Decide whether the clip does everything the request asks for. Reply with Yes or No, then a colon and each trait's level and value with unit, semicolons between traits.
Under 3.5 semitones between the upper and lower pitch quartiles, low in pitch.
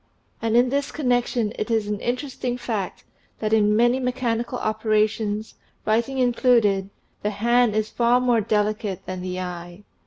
No: average, 2.8 semitones; high, 225 Hz